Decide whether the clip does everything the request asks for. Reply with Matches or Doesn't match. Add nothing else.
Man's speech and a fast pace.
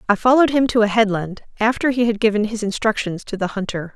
Doesn't match